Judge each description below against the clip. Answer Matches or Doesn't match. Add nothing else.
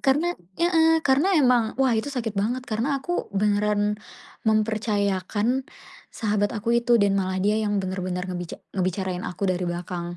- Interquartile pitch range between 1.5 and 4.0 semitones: Doesn't match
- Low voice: Doesn't match